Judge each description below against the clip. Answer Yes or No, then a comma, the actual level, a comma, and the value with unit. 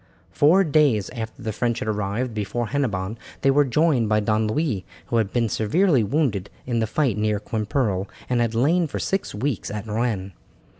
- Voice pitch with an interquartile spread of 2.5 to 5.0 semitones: Yes, average, 4.6 semitones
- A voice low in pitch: Yes, low, 115 Hz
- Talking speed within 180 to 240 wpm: Yes, average, 185 wpm